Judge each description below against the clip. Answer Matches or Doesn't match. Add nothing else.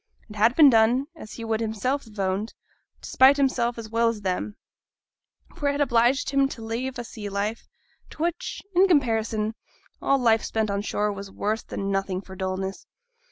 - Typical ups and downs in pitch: Matches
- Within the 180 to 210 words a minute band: Matches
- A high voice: Matches